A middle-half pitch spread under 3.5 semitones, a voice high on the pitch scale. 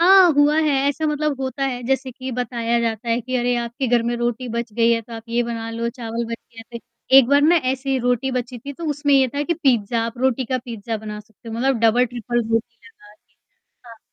Yes: narrow, 2.6 semitones; high, 240 Hz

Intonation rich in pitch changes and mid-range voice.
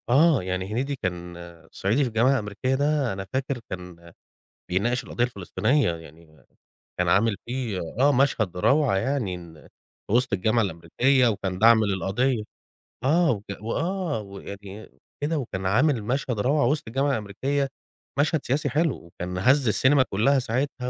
No: wide, 6.2 semitones; low, 120 Hz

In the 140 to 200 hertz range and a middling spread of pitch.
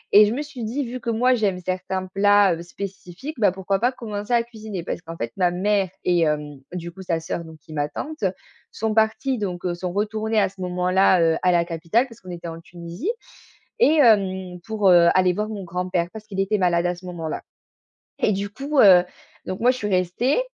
Yes: high, 190 Hz; average, 3.8 semitones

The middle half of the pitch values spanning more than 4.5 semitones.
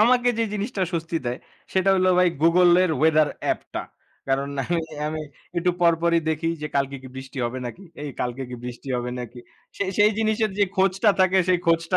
Yes: wide, 5.4 semitones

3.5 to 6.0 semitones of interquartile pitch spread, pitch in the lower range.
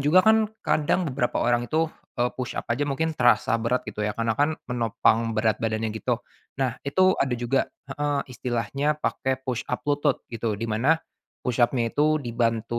Yes: average, 3.9 semitones; low, 125 Hz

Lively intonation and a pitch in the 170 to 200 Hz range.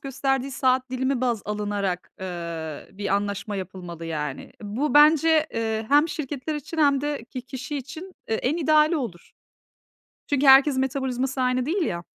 No: wide, 5.9 semitones; very high, 255 Hz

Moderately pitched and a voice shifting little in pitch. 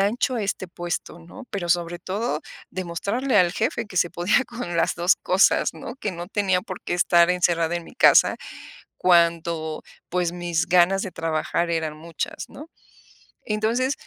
No: medium, 175 Hz; average, 3.3 semitones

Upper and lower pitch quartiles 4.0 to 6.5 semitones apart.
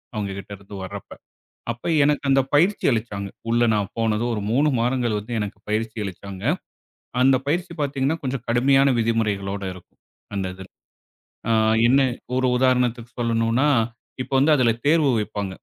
Yes: average, 4.4 semitones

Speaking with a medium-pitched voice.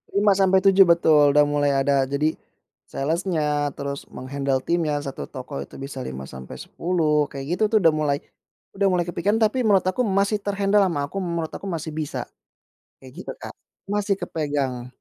Yes: medium, 160 Hz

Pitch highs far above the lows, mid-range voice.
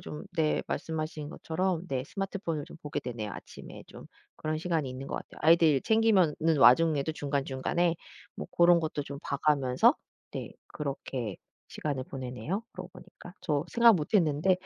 No: average, 3.7 semitones; medium, 155 Hz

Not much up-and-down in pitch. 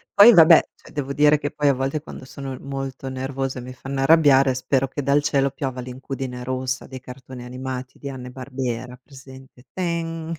Yes: narrow, 1.8 semitones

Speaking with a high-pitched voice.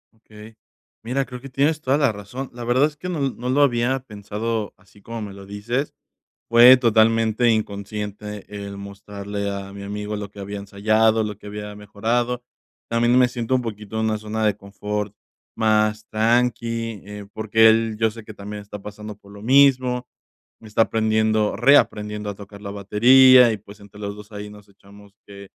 No: low, 110 Hz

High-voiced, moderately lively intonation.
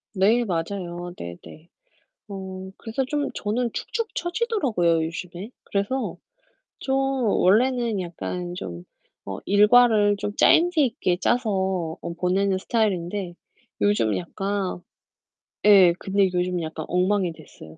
Yes: high, 195 Hz; average, 4.4 semitones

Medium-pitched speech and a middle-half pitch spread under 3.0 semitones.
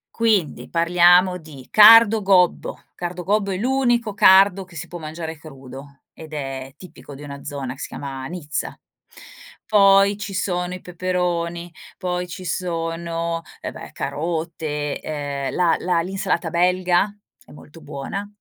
No: medium, 175 Hz; average, 3.5 semitones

